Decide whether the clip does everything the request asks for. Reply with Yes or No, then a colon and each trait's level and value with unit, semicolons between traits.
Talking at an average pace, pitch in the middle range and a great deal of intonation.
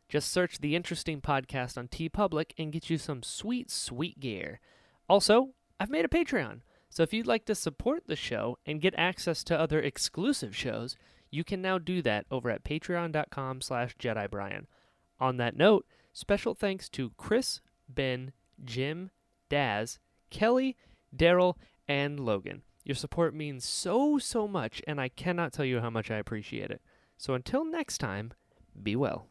Yes: average, 165 wpm; medium, 155 Hz; wide, 6.6 semitones